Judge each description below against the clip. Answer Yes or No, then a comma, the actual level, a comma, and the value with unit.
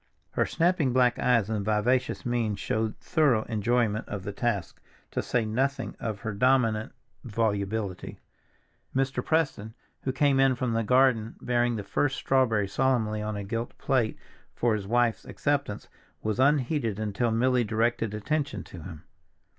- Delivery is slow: No, average, 150 wpm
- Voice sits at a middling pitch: No, low, 115 Hz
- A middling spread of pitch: Yes, average, 3.3 semitones